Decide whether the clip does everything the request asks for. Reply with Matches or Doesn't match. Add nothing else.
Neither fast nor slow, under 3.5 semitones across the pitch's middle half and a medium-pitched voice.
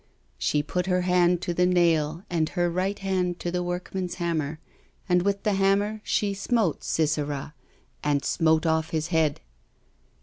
Matches